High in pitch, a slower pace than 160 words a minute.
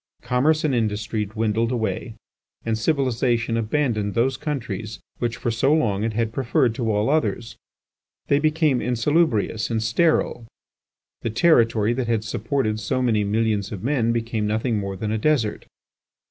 No: low, 115 Hz; average, 150 wpm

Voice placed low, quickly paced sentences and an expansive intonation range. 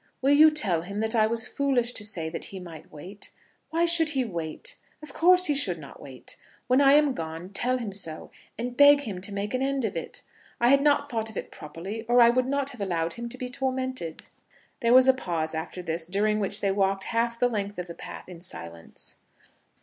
No: high, 225 Hz; fast, 225 wpm; wide, 6.5 semitones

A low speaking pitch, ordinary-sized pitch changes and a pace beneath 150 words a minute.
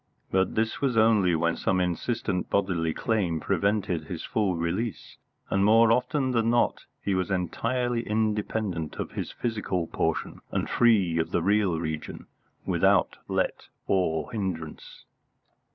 Yes: low, 100 Hz; average, 4.6 semitones; slow, 135 wpm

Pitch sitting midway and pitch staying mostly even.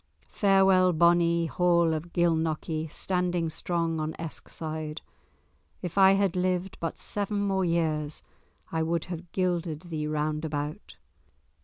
Yes: medium, 170 Hz; narrow, 2.3 semitones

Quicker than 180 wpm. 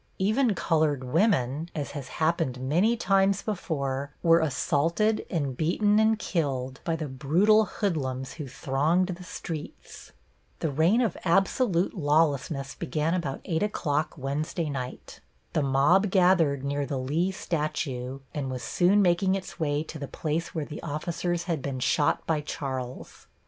No: average, 150 wpm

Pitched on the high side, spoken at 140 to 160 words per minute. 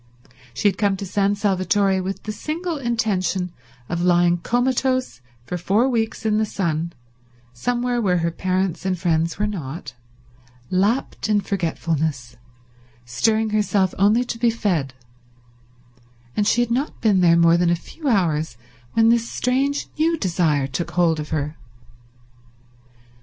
Yes: high, 195 Hz; average, 145 wpm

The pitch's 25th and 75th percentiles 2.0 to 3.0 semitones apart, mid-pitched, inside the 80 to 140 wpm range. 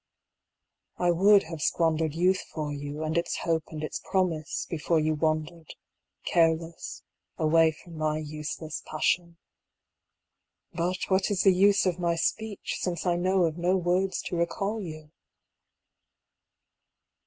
Yes: narrow, 2.6 semitones; medium, 170 Hz; slow, 135 wpm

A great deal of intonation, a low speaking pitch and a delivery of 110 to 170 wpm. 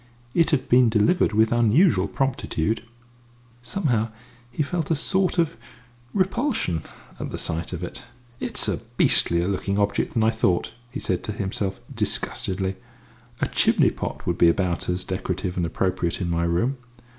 Yes: wide, 6.9 semitones; low, 105 Hz; average, 155 wpm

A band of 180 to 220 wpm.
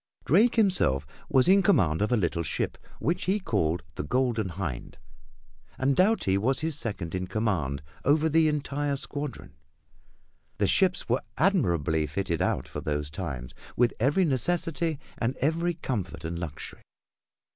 No: average, 145 wpm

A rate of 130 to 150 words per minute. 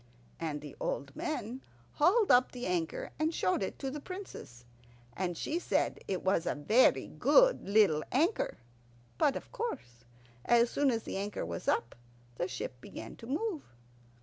No: average, 165 wpm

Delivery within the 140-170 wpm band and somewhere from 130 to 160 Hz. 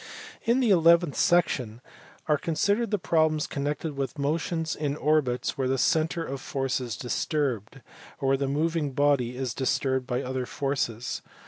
Yes: average, 155 wpm; medium, 140 Hz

